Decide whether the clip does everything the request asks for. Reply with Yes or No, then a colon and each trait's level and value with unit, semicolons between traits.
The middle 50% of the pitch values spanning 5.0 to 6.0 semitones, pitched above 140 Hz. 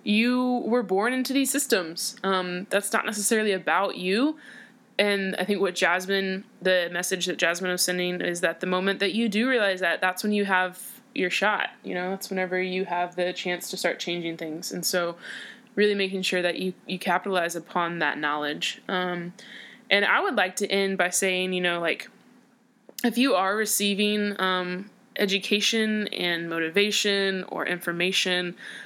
No: average, 2.8 semitones; high, 190 Hz